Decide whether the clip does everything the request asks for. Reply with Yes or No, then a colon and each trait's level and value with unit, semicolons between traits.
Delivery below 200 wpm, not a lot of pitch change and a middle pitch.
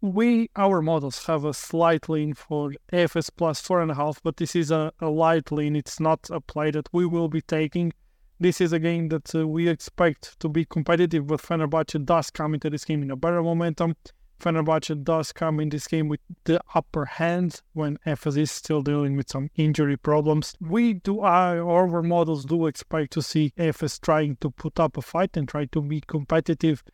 No: fast, 205 wpm; narrow, 1.8 semitones; medium, 160 Hz